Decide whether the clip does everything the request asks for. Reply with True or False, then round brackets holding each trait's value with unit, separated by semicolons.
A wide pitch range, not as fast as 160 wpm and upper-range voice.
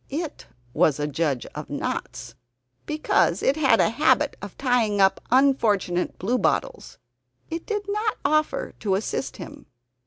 True (8.1 semitones; 135 wpm; 245 Hz)